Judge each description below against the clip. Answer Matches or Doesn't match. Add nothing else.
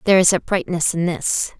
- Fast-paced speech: Doesn't match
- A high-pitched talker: Doesn't match